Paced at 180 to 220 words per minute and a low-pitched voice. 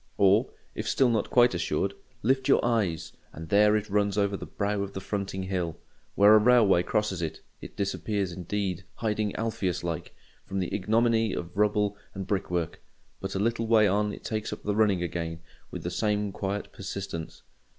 Yes: average, 185 wpm; low, 100 Hz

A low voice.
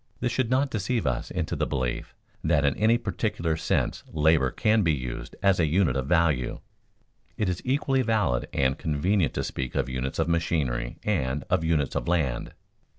Yes: very low, 80 Hz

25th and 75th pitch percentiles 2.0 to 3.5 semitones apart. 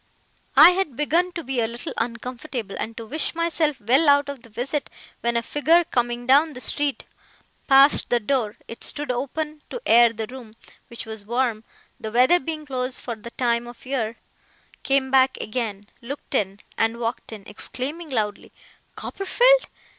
No: average, 4.1 semitones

